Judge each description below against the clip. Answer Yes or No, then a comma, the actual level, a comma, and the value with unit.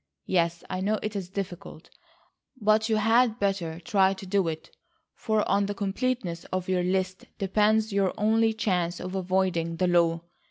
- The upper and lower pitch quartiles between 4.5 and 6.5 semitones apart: No, average, 3.0 semitones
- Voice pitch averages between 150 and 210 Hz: Yes, high, 190 Hz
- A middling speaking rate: Yes, average, 165 wpm